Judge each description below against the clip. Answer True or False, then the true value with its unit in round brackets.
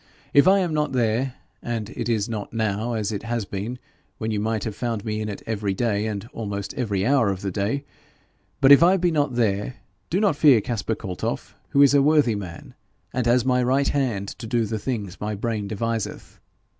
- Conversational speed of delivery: False (210 wpm)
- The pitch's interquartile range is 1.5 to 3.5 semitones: False (3.9 semitones)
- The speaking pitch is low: True (115 Hz)